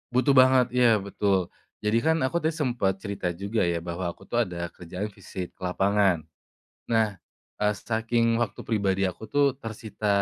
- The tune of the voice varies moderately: Yes, average, 3.7 semitones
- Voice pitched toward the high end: No, low, 105 Hz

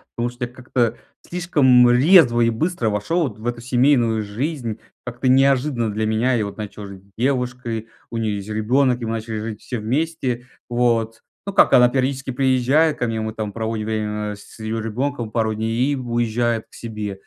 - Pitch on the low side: Yes, low, 120 Hz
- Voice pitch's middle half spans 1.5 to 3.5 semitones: Yes, average, 2.8 semitones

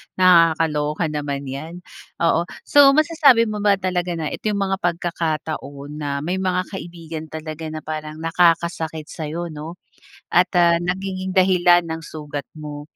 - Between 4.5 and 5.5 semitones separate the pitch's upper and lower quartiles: No, average, 2.9 semitones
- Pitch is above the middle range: No, medium, 165 Hz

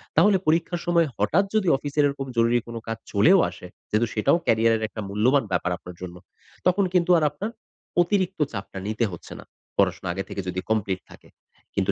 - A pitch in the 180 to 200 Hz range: No, low, 115 Hz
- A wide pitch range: Yes, wide, 9.0 semitones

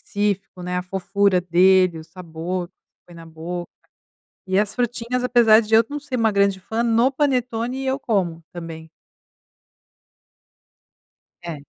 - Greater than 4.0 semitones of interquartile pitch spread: Yes, average, 4.9 semitones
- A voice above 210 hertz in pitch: No, high, 195 Hz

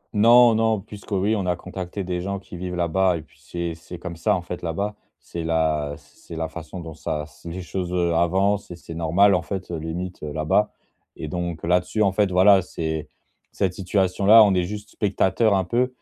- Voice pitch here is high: No, very low, 90 Hz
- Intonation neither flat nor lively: Yes, average, 3.0 semitones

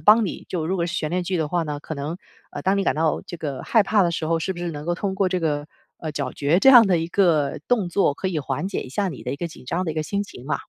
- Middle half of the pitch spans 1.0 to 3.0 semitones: No, average, 3.9 semitones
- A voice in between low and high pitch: Yes, medium, 170 Hz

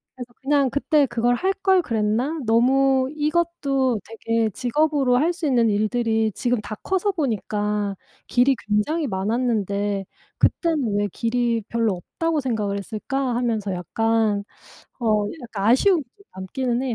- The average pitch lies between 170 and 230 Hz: No, high, 240 Hz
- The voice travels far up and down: No, average, 4.4 semitones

